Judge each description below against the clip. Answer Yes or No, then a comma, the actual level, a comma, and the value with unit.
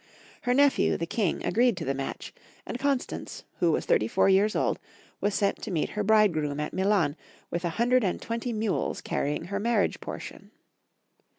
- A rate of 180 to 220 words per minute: Yes, average, 185 wpm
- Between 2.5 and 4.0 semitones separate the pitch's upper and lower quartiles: No, wide, 5.6 semitones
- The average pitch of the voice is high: Yes, high, 200 Hz